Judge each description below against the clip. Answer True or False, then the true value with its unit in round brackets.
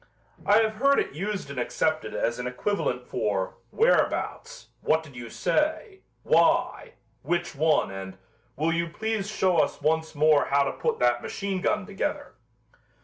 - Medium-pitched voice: True (160 Hz)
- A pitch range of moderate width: False (8.5 semitones)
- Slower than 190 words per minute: True (155 wpm)